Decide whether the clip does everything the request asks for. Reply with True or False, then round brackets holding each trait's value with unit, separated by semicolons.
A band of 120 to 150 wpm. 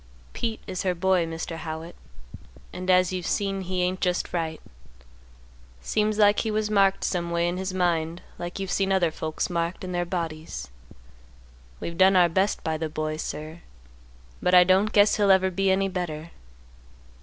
False (175 wpm)